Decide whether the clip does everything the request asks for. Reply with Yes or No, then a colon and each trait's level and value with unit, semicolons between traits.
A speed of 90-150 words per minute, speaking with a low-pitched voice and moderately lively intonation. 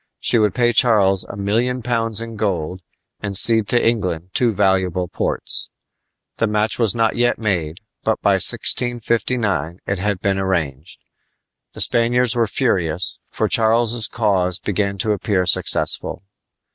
Yes: average, 145 wpm; low, 105 Hz; average, 3.6 semitones